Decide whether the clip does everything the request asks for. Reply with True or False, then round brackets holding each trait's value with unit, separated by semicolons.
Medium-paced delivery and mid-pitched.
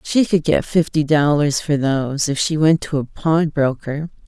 True (185 wpm; 150 Hz)